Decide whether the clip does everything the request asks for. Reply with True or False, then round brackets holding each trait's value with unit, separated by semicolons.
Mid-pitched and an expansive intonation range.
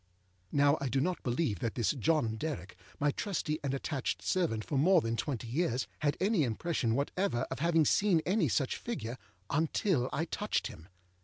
True (145 Hz; 5.7 semitones)